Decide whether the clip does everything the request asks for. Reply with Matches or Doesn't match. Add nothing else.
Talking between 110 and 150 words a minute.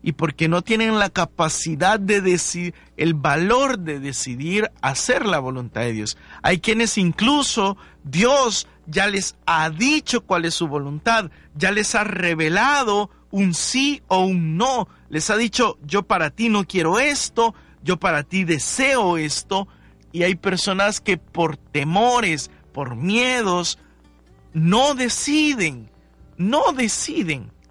Matches